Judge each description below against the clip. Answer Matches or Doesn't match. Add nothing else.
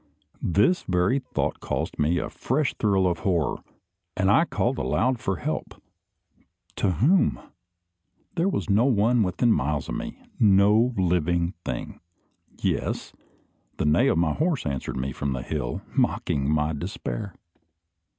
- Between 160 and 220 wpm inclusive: Doesn't match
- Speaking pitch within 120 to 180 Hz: Doesn't match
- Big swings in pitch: Matches